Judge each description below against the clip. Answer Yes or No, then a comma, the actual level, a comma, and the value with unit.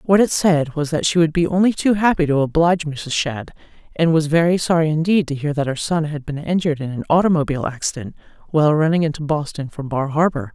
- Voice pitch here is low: No, medium, 155 Hz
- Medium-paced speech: No, fast, 220 wpm